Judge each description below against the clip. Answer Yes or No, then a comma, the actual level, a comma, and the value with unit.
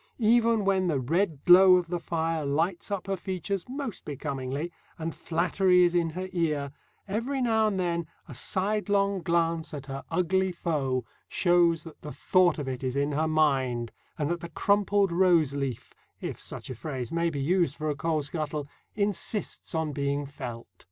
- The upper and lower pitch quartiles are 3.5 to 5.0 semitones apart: Yes, average, 4.6 semitones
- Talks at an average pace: Yes, average, 175 wpm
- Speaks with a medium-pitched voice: Yes, medium, 170 Hz